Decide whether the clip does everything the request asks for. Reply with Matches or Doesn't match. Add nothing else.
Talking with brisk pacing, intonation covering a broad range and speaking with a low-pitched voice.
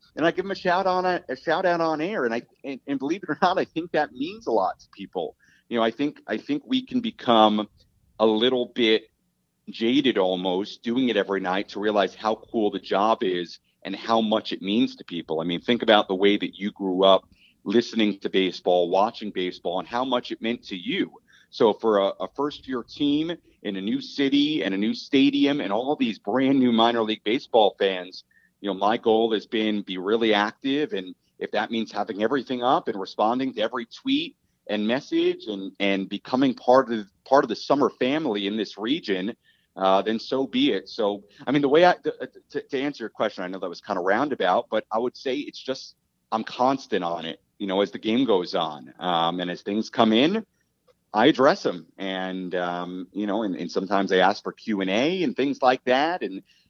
Matches